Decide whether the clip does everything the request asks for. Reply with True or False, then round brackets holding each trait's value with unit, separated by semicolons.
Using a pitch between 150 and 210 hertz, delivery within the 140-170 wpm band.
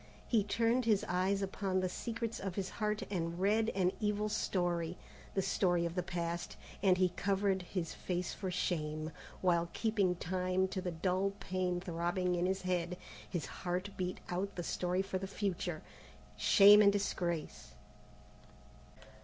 True (185 Hz; 155 wpm)